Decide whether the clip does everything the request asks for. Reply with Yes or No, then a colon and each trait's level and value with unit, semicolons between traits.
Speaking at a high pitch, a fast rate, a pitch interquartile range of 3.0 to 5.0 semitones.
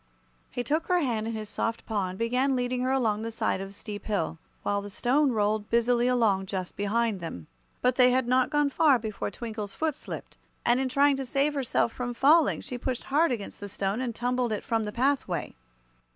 Yes: high, 240 Hz; fast, 215 wpm; average, 3.7 semitones